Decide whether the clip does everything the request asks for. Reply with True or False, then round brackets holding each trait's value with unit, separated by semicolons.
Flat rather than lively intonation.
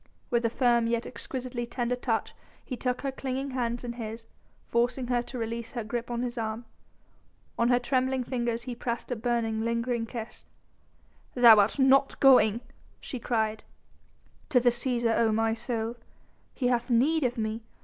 True (1.5 semitones)